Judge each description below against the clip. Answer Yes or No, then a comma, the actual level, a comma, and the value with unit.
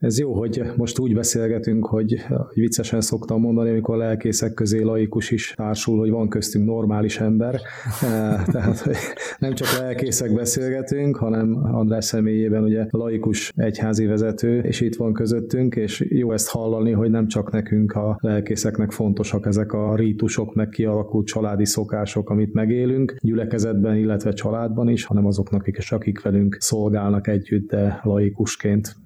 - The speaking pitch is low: Yes, low, 110 Hz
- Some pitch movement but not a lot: No, narrow, 1.4 semitones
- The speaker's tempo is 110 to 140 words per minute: No, average, 150 wpm